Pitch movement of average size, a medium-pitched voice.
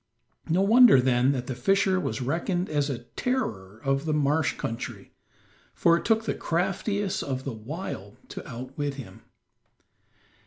No: wide, 6.6 semitones; medium, 145 Hz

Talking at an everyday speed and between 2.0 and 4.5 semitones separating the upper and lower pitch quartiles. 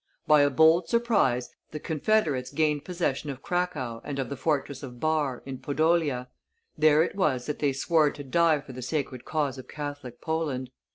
Yes: average, 180 wpm; average, 3.3 semitones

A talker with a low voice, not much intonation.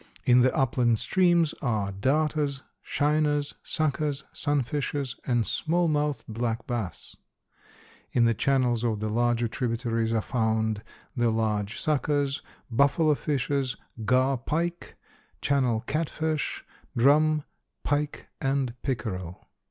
No: low, 130 Hz; average, 4.2 semitones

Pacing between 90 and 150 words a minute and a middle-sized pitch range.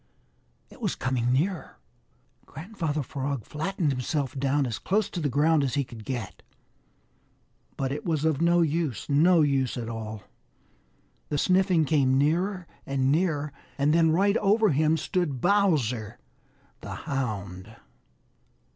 Yes: average, 140 wpm; average, 4.4 semitones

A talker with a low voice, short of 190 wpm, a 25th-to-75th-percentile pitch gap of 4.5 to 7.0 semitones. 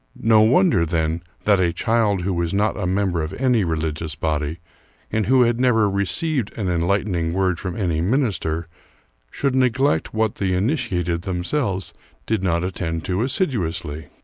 Yes: very low, 95 Hz; average, 155 wpm; average, 4.9 semitones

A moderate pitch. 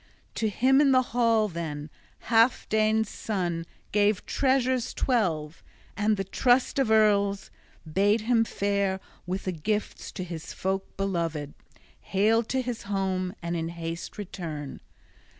No: high, 200 Hz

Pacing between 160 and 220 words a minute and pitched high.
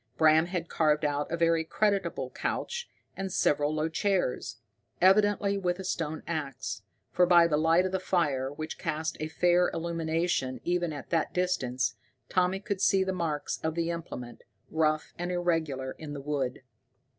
No: average, 165 wpm; medium, 165 Hz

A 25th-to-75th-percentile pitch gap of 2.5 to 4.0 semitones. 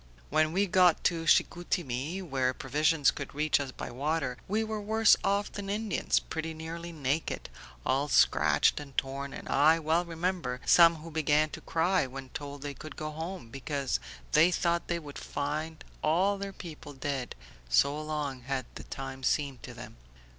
Yes: average, 3.6 semitones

